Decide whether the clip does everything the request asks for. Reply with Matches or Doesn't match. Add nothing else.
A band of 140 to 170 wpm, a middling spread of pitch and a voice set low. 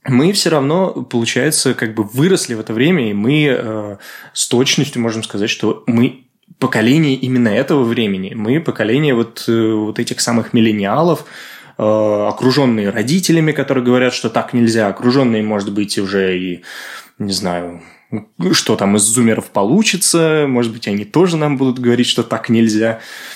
Matches